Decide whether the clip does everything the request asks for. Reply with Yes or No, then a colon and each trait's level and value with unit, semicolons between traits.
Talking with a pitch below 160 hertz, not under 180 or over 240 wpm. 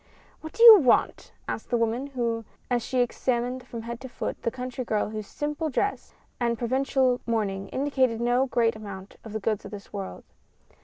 No: high, 240 Hz; average, 185 wpm